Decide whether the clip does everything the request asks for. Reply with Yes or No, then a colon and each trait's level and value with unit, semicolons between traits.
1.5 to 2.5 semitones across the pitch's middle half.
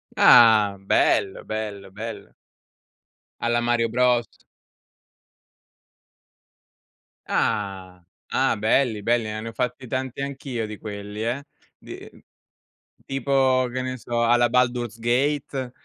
No: average, 2.9 semitones